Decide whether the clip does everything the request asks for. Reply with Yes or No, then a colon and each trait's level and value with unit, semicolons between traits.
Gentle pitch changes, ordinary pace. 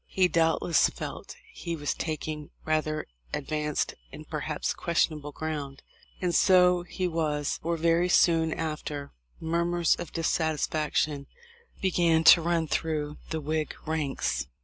No: narrow, 2.0 semitones; slow, 125 wpm